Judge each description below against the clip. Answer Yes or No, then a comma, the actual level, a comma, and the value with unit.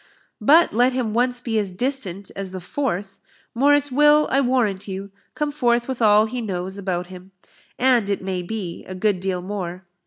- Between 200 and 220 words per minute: No, average, 185 wpm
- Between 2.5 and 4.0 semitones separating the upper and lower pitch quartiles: No, average, 5.1 semitones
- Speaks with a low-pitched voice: No, high, 210 Hz